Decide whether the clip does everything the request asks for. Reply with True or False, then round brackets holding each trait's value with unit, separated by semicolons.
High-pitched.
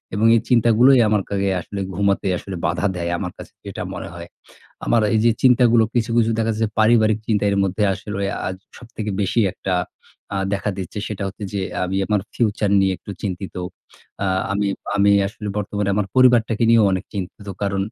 False (105 Hz)